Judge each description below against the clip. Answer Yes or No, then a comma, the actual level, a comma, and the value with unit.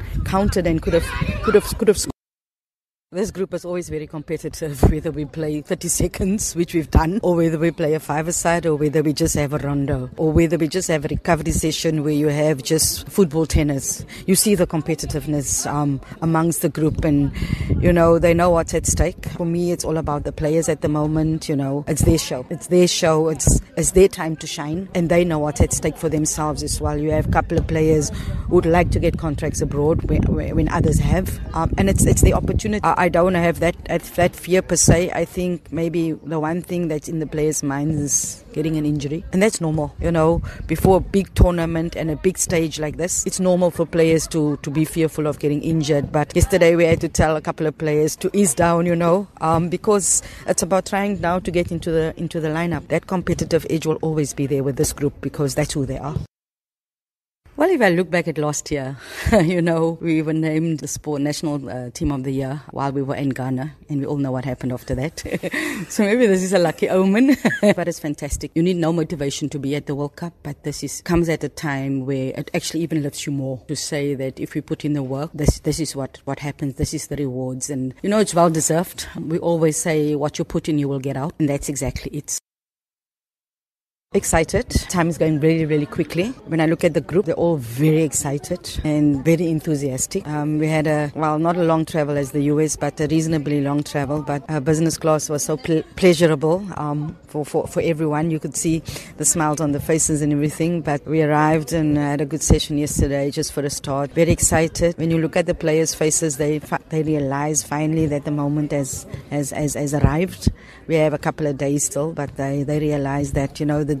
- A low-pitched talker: No, medium, 155 Hz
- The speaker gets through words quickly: Yes, fast, 230 wpm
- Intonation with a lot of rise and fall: No, narrow, 2.5 semitones